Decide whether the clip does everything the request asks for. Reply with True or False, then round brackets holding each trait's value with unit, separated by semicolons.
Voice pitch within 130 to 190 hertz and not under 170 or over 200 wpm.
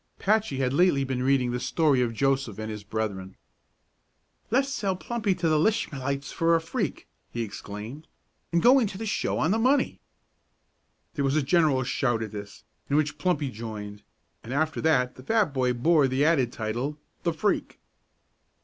True (140 Hz; 175 wpm)